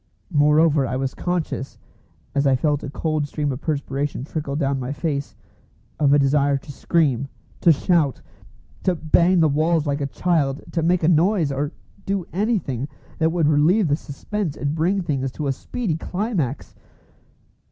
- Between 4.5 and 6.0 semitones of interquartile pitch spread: No, average, 3.3 semitones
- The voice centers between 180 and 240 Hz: No, medium, 150 Hz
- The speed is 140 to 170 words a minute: Yes, average, 165 wpm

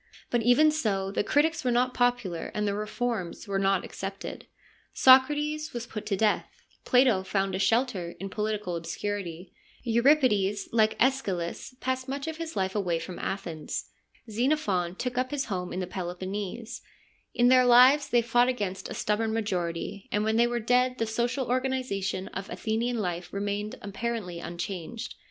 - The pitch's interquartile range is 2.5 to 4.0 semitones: No, average, 4.5 semitones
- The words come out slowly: No, average, 160 wpm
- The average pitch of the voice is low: No, high, 215 Hz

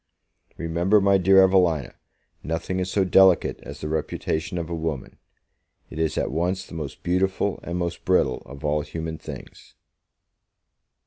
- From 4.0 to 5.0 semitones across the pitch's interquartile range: No, average, 3.0 semitones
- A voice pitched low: Yes, very low, 85 Hz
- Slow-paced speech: No, average, 150 wpm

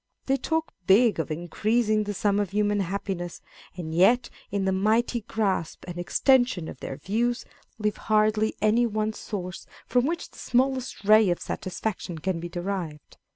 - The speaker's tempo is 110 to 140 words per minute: No, average, 160 wpm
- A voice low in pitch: No, high, 205 Hz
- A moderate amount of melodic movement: Yes, average, 4.0 semitones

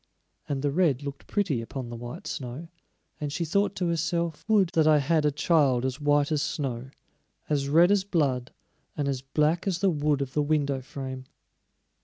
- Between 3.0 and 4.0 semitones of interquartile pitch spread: Yes, average, 3.6 semitones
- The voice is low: No, medium, 145 Hz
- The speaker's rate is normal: Yes, average, 190 wpm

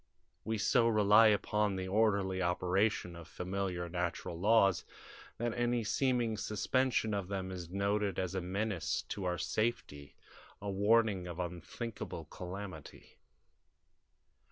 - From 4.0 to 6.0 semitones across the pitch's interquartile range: No, average, 3.3 semitones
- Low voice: Yes, low, 100 Hz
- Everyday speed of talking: No, slow, 125 wpm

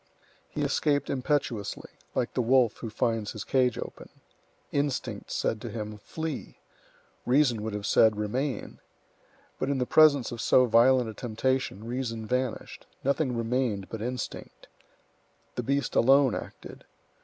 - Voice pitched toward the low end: Yes, low, 125 Hz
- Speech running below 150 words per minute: Yes, average, 140 wpm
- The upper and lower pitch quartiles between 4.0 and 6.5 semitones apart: No, average, 3.1 semitones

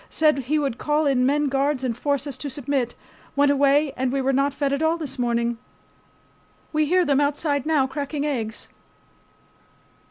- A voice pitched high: Yes, very high, 280 Hz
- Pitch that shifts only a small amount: Yes, narrow, 2.0 semitones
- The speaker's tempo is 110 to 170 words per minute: No, average, 180 wpm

